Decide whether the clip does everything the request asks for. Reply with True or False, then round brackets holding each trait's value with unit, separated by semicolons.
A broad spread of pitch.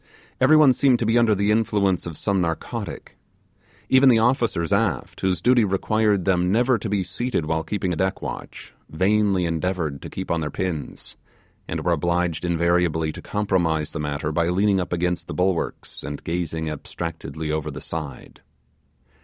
False (4.3 semitones)